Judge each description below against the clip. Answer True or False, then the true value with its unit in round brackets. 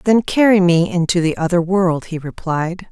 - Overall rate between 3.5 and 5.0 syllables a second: True (4.7 syllables/s)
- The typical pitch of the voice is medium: True (180 Hz)